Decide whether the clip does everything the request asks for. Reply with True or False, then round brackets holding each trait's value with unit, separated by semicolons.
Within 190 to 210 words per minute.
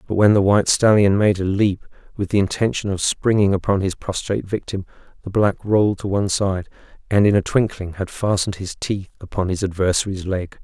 True (195 wpm)